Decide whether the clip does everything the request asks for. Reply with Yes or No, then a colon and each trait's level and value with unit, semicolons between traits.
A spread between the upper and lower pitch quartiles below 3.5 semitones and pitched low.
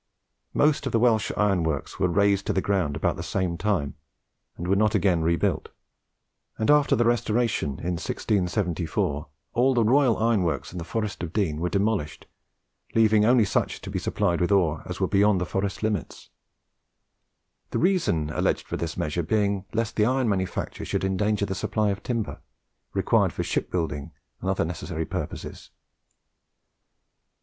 No: average, 4.3 semitones; low, 100 Hz